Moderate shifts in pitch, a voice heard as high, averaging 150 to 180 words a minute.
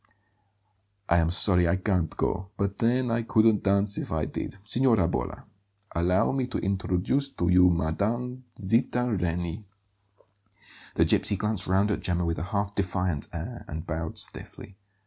No: average, 4.0 semitones; very low, 95 Hz; average, 155 wpm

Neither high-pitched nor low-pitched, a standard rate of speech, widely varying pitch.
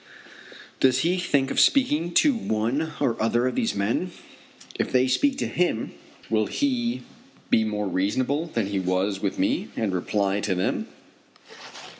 No: low, 120 Hz; average, 160 wpm; wide, 8.6 semitones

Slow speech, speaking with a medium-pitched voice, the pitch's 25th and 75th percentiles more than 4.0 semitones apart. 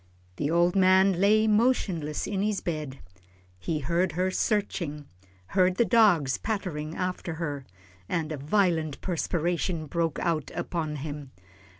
No: slow, 130 wpm; medium, 170 Hz; average, 3.7 semitones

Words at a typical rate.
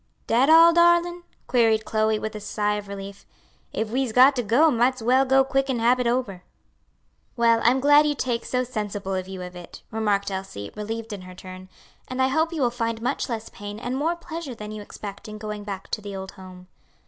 No: fast, 220 wpm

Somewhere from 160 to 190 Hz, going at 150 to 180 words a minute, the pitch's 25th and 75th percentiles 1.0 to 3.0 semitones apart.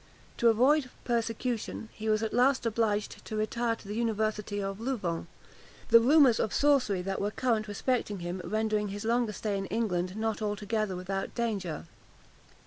No: high, 215 Hz; average, 160 wpm; narrow, 2.5 semitones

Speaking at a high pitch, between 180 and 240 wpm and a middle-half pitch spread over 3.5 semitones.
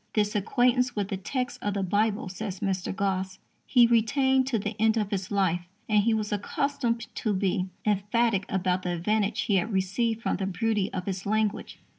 No: high, 205 Hz; average, 190 wpm; average, 2.8 semitones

